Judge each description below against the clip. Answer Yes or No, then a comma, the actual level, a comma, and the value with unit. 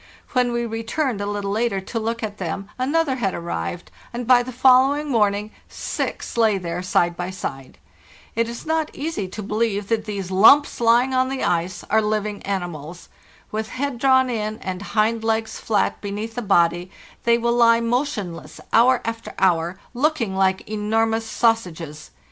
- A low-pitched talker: No, high, 220 Hz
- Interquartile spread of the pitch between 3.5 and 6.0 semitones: Yes, average, 3.9 semitones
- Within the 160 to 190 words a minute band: Yes, average, 170 wpm